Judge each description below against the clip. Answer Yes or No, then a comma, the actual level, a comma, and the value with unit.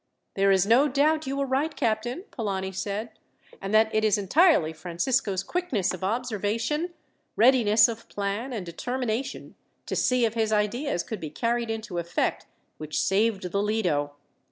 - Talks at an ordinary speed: Yes, average, 155 wpm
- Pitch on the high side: Yes, high, 220 Hz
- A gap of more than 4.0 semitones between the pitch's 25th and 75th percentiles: Yes, average, 4.5 semitones